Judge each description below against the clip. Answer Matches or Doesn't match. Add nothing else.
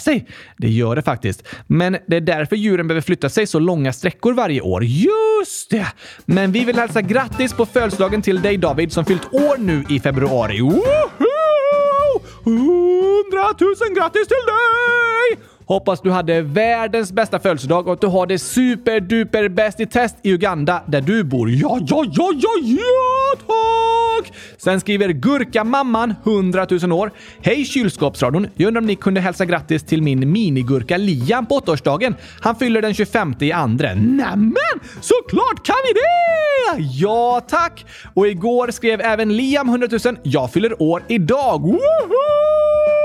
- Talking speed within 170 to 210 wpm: Doesn't match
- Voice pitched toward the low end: Doesn't match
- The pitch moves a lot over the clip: Matches